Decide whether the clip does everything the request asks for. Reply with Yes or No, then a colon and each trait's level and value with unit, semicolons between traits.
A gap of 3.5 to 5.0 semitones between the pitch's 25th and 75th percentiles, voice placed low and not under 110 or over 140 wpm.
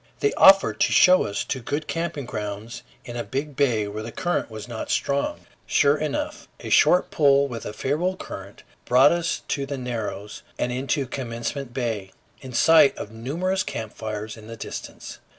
No: average, 4.6 semitones; low, 130 Hz; average, 180 wpm